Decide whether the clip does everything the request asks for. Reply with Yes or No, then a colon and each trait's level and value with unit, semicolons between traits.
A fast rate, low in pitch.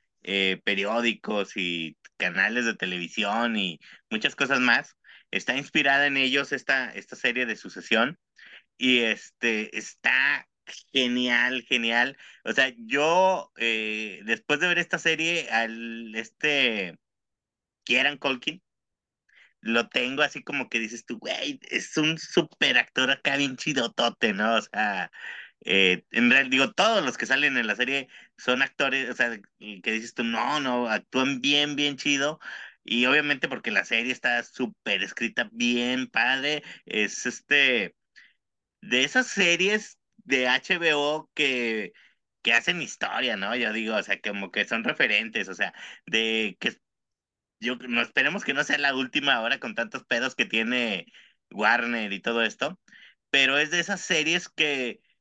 No: average, 150 wpm; low, 125 Hz